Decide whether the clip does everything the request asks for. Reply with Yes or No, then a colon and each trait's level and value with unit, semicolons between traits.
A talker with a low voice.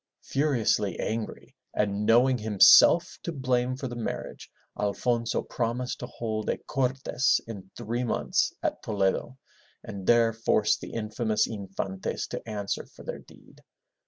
Yes: low, 115 Hz